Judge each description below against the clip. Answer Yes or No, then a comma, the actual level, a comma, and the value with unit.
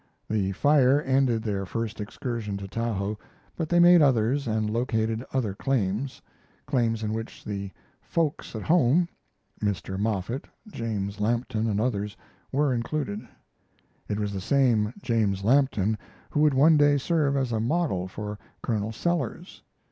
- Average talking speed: Yes, average, 145 wpm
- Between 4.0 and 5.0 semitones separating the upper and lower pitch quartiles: Yes, average, 4.7 semitones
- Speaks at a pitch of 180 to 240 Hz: No, low, 115 Hz